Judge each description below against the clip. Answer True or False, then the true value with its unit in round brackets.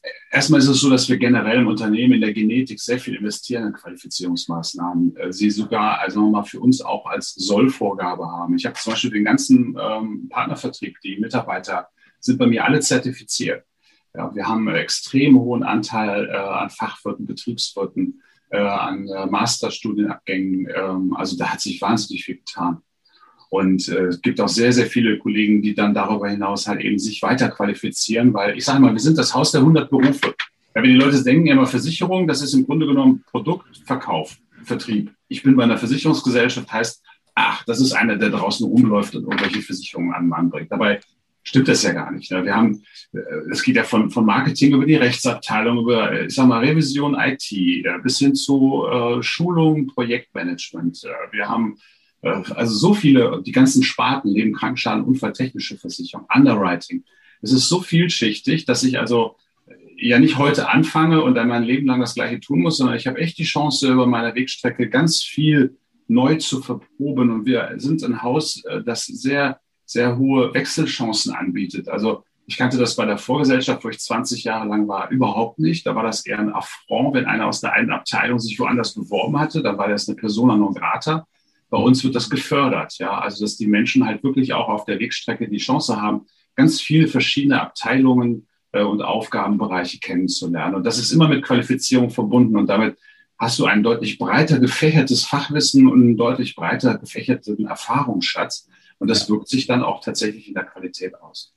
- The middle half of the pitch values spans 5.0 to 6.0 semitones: True (5.4 semitones)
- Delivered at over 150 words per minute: True (185 wpm)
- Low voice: True (130 Hz)